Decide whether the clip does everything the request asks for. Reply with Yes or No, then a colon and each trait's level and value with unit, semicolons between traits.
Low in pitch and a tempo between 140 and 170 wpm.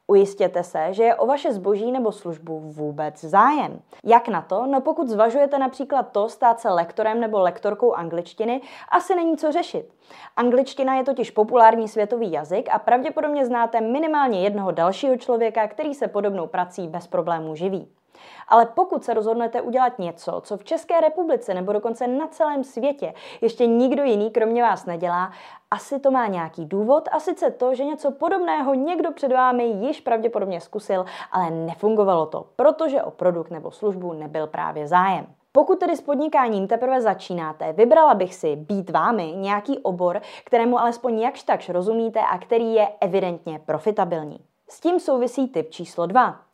No: high, 230 Hz; average, 165 wpm